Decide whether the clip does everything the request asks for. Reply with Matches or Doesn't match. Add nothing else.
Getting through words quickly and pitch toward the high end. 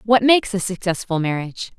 Doesn't match